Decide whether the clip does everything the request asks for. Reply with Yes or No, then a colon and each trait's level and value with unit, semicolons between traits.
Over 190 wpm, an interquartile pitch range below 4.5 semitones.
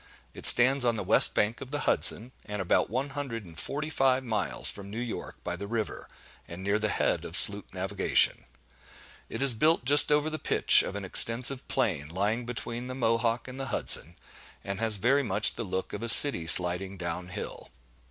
No: average, 200 wpm; average, 4.8 semitones